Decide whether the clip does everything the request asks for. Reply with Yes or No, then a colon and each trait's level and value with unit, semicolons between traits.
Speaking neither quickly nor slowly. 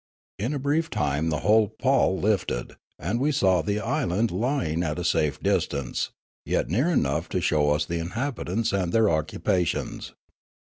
Yes: average, 170 wpm